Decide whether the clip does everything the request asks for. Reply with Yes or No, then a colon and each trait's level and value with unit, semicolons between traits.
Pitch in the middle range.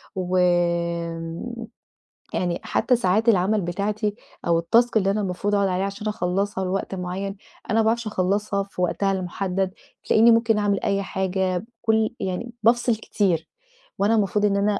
No: high, 195 Hz